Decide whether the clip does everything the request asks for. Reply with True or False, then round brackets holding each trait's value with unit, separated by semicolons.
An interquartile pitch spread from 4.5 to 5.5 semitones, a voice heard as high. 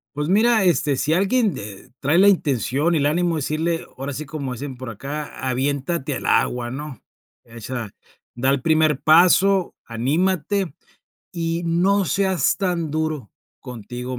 False (5.0 semitones; 150 Hz)